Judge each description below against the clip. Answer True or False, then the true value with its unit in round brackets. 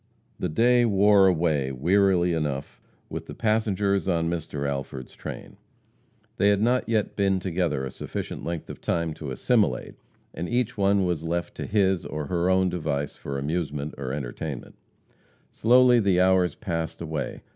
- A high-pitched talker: False (85 Hz)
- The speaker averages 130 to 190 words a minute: True (155 wpm)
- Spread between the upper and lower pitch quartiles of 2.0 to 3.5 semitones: False (4.6 semitones)